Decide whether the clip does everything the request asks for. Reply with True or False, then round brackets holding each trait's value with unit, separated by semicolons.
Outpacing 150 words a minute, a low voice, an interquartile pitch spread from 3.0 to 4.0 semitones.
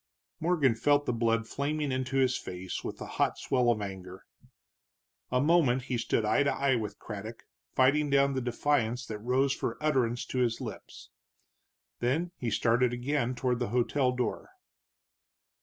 True (160 wpm; 125 Hz; 3.3 semitones)